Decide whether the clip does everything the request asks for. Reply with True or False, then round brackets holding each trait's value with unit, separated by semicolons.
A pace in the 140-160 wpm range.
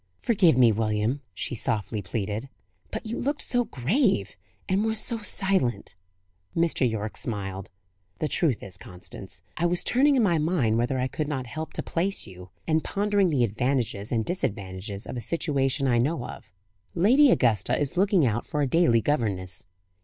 False (170 wpm)